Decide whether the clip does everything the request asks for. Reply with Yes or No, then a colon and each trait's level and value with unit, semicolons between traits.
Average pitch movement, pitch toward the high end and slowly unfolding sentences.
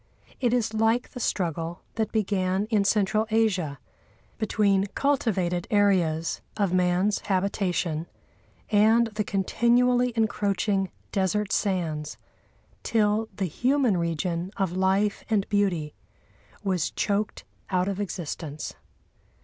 Yes: average, 3.3 semitones; high, 200 Hz; slow, 110 wpm